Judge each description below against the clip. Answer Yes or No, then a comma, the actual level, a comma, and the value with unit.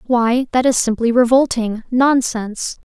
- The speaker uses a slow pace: Yes, slow, 125 wpm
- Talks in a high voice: Yes, high, 240 Hz